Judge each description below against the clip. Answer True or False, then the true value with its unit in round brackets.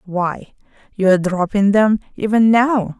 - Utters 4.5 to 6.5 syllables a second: False (4.3 syllables/s)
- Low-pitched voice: False (205 Hz)